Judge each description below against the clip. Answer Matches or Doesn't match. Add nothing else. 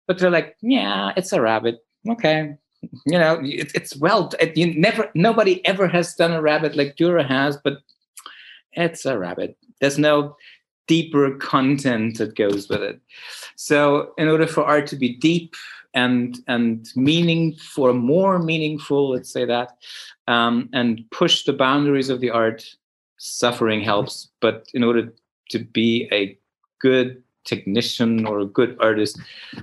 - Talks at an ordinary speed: Matches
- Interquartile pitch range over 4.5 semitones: Matches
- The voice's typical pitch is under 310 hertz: Matches